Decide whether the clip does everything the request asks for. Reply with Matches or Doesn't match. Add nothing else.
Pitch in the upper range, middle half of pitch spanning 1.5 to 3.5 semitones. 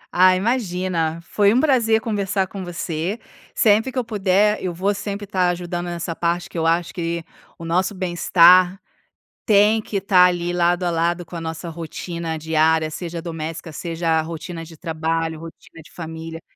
Doesn't match